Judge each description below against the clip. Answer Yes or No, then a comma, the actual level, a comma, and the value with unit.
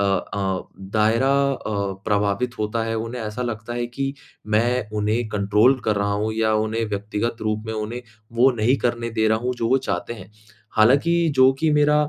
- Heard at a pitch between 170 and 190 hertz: No, low, 110 Hz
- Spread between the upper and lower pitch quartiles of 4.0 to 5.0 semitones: No, narrow, 2.6 semitones